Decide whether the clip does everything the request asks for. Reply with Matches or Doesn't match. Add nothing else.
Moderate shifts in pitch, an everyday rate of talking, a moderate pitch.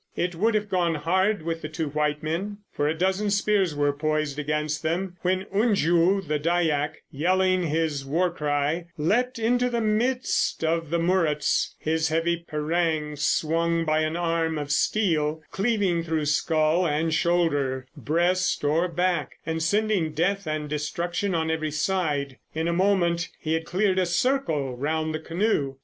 Matches